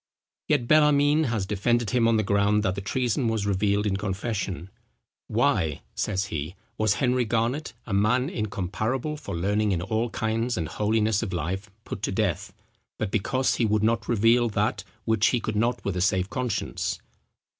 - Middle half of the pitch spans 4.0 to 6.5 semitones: No, average, 3.2 semitones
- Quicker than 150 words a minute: Yes, average, 175 wpm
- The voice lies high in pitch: No, low, 110 Hz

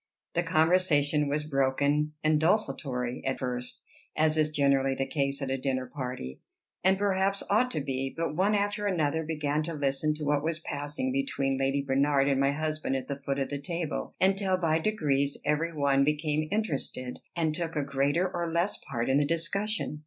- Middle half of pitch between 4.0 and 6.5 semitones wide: No, average, 3.4 semitones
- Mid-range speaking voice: Yes, medium, 150 Hz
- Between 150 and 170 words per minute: No, average, 185 wpm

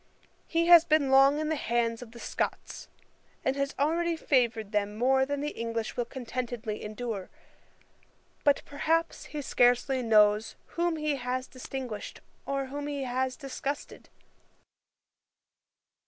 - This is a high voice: Yes, very high, 265 Hz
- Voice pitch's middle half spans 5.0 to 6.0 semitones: No, average, 3.6 semitones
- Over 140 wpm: No, slow, 135 wpm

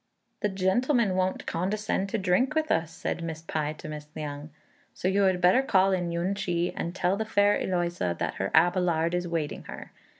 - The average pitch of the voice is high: No, medium, 180 Hz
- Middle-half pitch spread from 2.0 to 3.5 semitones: Yes, average, 2.9 semitones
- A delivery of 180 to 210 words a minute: Yes, average, 195 wpm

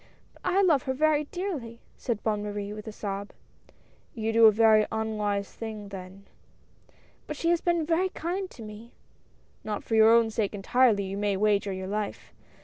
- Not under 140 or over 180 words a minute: No, average, 190 wpm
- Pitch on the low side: No, high, 220 Hz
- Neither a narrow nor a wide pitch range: Yes, average, 4.7 semitones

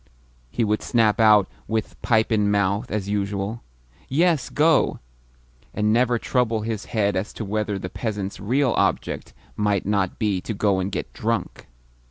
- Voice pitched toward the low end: Yes, low, 105 Hz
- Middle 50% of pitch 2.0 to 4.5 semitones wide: Yes, narrow, 2.4 semitones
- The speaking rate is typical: Yes, average, 160 wpm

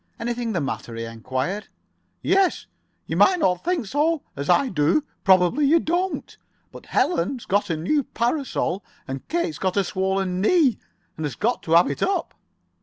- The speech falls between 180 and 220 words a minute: No, average, 170 wpm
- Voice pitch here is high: Yes, high, 205 Hz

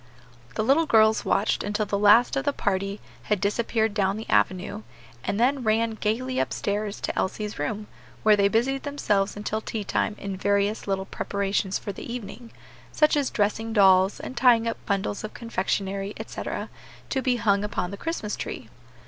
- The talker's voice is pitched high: Yes, high, 210 Hz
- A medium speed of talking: Yes, average, 175 wpm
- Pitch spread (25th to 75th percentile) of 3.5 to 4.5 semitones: No, narrow, 2.5 semitones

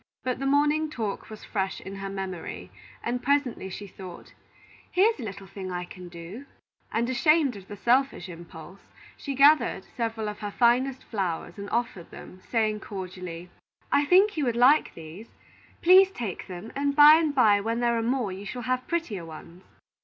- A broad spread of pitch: Yes, wide, 6.2 semitones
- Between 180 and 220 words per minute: Yes, average, 185 wpm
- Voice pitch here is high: Yes, high, 225 Hz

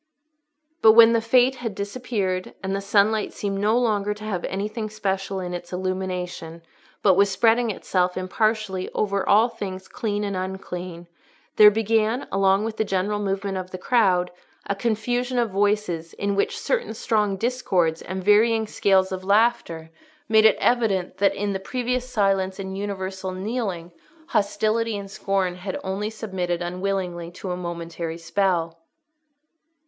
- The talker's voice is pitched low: No, high, 200 Hz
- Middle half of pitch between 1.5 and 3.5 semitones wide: Yes, average, 2.7 semitones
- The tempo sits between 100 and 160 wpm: Yes, average, 155 wpm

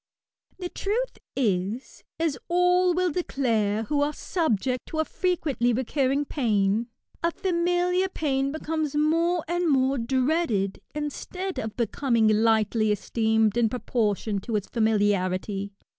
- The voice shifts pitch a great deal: Yes, wide, 7.2 semitones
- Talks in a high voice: Yes, very high, 265 Hz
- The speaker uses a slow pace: Yes, slow, 125 wpm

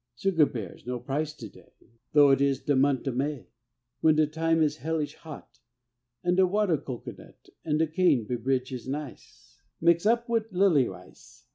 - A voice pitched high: No, medium, 150 Hz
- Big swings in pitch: No, average, 3.7 semitones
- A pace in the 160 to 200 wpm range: Yes, average, 180 wpm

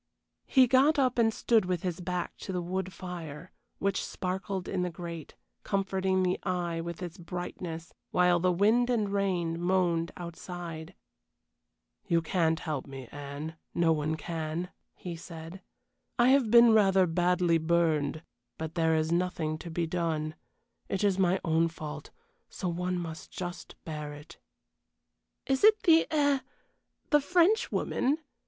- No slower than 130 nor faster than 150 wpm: Yes, average, 145 wpm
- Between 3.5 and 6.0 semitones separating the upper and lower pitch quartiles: No, average, 2.9 semitones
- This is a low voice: No, medium, 175 Hz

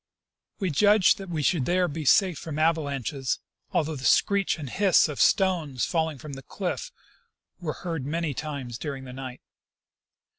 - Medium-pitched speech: Yes, medium, 155 Hz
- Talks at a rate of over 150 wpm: Yes, average, 160 wpm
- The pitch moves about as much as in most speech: Yes, average, 4.4 semitones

